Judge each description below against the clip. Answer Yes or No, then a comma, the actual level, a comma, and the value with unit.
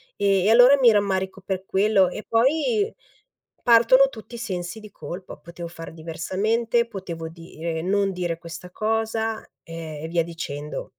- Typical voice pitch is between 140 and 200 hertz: Yes, high, 190 Hz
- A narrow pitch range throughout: No, average, 4.9 semitones